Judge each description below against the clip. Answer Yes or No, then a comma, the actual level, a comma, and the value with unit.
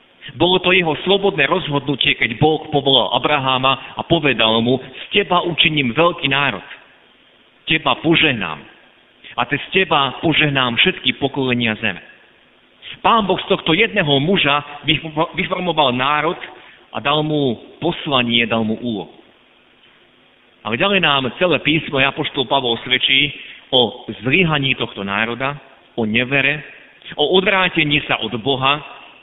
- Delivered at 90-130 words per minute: Yes, average, 125 wpm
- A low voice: No, medium, 145 Hz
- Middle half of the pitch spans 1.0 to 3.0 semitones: No, average, 4.3 semitones